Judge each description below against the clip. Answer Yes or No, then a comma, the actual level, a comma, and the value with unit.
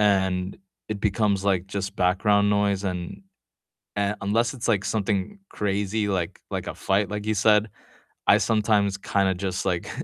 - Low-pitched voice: Yes, low, 100 Hz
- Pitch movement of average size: No, narrow, 1.7 semitones